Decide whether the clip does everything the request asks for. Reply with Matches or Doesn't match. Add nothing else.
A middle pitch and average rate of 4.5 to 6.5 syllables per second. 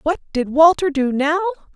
Doesn't match